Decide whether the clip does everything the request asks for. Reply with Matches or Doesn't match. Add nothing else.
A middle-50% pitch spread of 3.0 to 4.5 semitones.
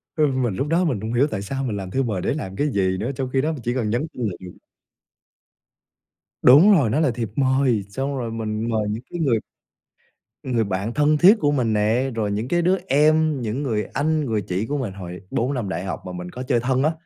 Doesn't match